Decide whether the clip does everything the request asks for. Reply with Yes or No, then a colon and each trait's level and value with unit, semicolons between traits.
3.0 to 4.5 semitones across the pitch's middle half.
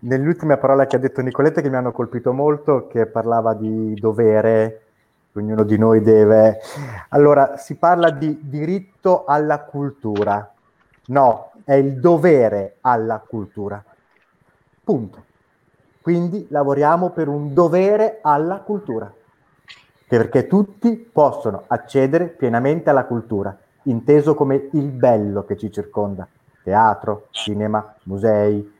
No: average, 5.3 semitones